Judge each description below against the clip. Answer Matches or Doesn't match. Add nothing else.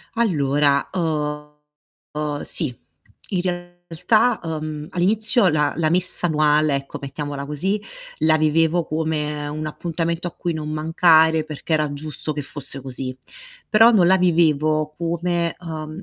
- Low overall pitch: Doesn't match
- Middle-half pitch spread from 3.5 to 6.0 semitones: Doesn't match